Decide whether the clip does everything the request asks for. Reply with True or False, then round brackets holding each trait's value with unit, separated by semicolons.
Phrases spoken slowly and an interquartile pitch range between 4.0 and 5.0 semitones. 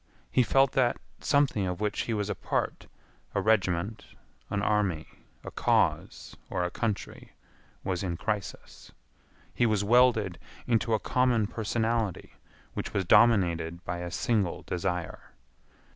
True (130 wpm; 4.3 semitones)